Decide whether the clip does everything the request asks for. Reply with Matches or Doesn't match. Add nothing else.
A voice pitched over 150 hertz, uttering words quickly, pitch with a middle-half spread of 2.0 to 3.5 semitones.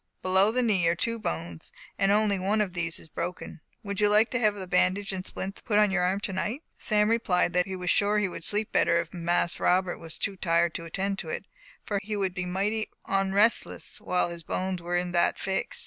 Matches